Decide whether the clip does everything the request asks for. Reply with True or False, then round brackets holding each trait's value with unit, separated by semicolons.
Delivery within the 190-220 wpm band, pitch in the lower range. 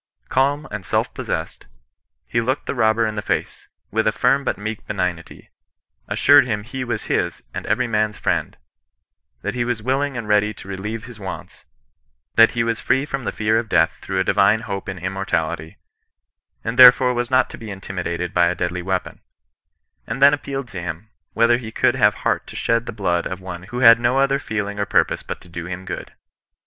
True (205 wpm; 110 Hz)